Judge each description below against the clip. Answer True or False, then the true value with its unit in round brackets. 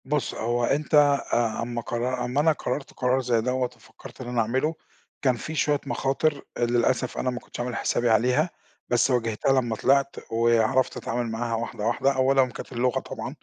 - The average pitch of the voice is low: True (125 Hz)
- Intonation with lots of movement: False (2.4 semitones)